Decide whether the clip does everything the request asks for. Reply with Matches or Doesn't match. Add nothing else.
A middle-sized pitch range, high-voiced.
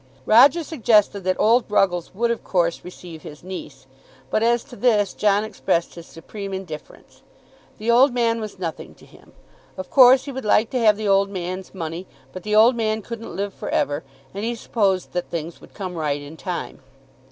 Matches